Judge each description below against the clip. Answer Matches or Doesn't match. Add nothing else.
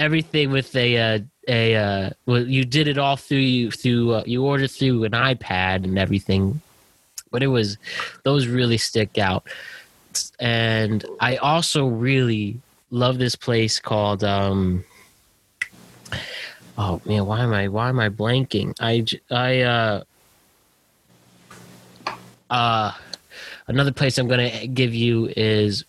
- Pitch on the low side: Matches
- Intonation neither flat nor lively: Matches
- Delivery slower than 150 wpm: Matches